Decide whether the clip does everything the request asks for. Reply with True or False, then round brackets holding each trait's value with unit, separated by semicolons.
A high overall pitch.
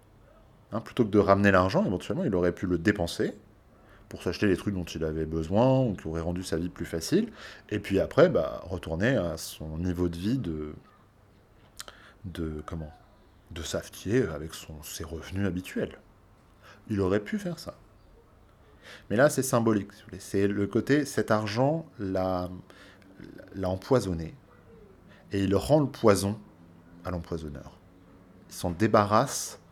False (95 Hz)